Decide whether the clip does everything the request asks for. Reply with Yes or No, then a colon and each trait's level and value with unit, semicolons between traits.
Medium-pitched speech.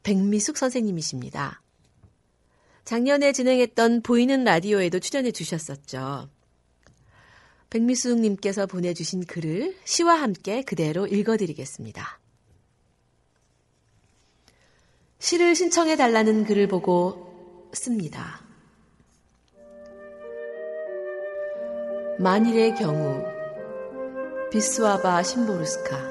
No: high, 200 Hz